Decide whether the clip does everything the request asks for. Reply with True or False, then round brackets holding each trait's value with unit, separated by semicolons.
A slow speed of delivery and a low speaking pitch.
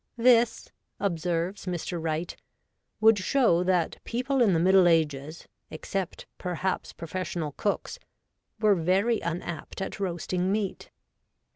False (120 wpm; 185 Hz)